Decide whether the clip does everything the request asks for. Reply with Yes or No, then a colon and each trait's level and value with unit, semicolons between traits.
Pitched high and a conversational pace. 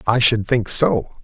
No: low, 115 Hz; average, 195 wpm